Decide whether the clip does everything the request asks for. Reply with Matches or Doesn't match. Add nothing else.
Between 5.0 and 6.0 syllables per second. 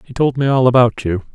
Matches